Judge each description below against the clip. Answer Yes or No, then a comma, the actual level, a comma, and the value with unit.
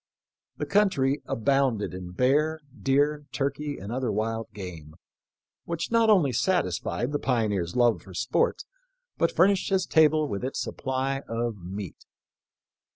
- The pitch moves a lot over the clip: Yes, wide, 6.2 semitones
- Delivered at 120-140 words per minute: Yes, slow, 135 wpm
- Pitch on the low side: Yes, low, 130 Hz